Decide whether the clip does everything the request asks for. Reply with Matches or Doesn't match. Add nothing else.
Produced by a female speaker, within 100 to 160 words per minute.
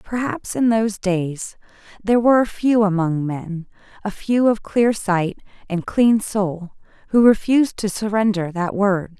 Matches